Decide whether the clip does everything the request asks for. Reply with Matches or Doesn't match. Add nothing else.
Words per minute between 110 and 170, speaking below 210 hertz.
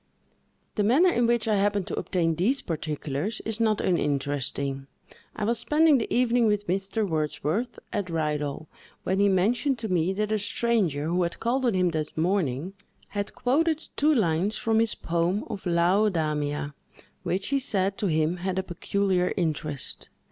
Matches